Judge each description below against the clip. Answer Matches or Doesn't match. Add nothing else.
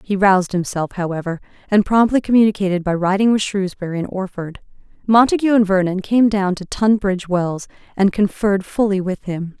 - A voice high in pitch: Matches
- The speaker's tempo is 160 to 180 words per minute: Matches